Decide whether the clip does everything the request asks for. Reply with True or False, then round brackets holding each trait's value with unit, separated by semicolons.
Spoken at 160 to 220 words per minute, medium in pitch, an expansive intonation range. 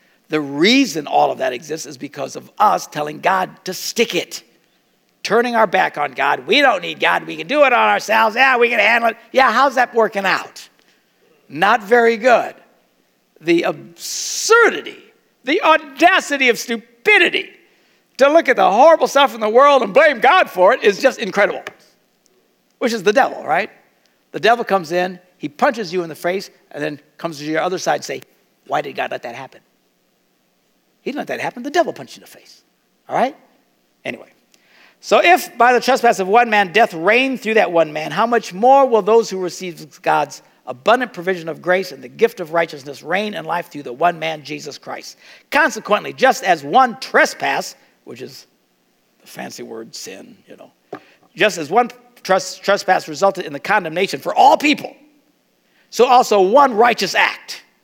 False (190 wpm; 230 Hz; 6.3 semitones)